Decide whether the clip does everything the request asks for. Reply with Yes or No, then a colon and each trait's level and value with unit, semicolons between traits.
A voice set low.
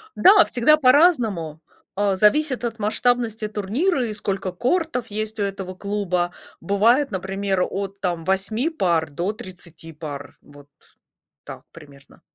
No: high, 200 Hz